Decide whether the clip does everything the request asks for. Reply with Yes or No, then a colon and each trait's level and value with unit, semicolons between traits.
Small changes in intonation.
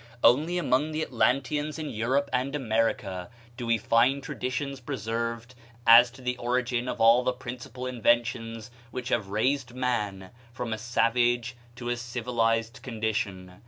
Yes: narrow, 2.0 semitones